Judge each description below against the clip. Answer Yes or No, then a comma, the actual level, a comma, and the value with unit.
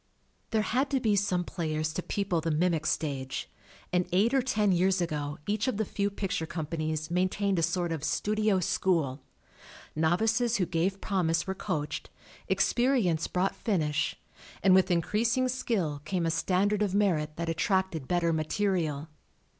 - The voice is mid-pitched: Yes, medium, 180 Hz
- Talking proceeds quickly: No, average, 160 wpm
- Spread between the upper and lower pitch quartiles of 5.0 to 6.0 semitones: No, average, 4.2 semitones